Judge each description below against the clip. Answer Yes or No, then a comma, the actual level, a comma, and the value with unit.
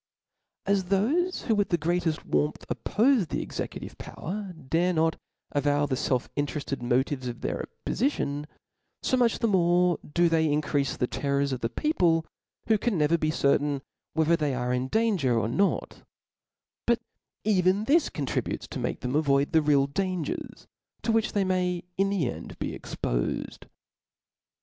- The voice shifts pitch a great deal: Yes, wide, 5.7 semitones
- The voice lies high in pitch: No, medium, 165 Hz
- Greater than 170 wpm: No, average, 165 wpm